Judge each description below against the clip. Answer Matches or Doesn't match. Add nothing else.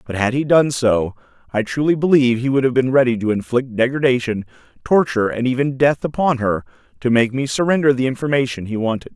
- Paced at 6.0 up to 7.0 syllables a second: Matches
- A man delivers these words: Matches